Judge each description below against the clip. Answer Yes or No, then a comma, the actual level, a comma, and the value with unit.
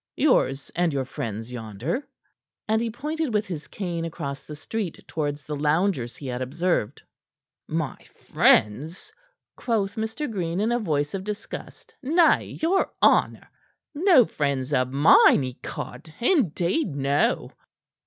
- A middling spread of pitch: No, wide, 7.9 semitones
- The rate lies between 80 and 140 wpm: Yes, slow, 135 wpm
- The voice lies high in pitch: No, medium, 165 Hz